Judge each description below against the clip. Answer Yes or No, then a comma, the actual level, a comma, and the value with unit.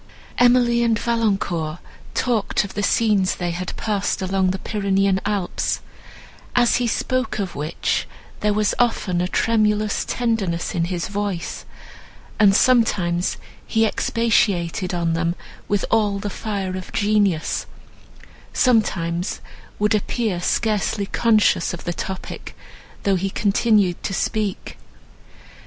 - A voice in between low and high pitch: No, high, 200 Hz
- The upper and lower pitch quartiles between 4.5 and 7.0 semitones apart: No, average, 3.4 semitones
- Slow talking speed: Yes, slow, 125 wpm